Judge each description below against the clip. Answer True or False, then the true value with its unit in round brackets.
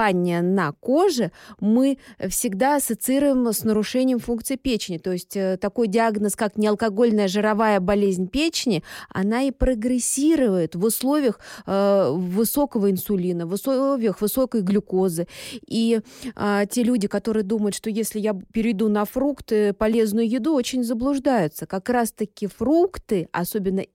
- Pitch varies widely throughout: False (3.9 semitones)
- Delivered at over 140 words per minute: False (125 wpm)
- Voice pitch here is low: False (220 Hz)